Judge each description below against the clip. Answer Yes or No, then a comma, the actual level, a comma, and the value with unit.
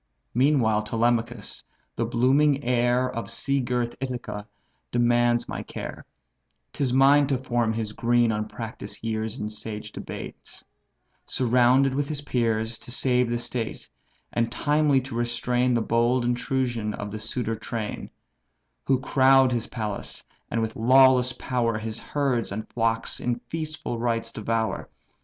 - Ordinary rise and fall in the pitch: No, narrow, 2.3 semitones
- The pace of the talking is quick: No, average, 140 wpm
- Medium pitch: No, low, 120 Hz